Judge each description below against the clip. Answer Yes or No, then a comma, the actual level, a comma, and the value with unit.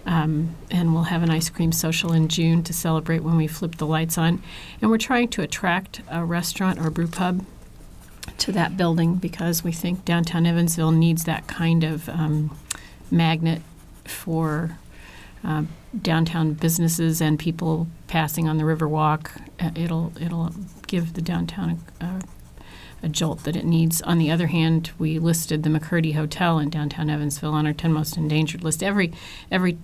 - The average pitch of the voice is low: No, medium, 165 Hz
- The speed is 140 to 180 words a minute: Yes, average, 170 wpm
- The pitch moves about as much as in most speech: No, narrow, 1.3 semitones